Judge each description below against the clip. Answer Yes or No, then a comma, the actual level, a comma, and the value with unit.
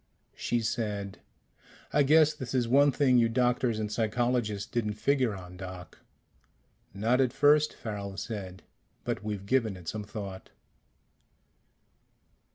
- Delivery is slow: Yes, slow, 130 wpm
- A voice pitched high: No, low, 110 Hz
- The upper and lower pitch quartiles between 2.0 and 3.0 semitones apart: No, average, 4.0 semitones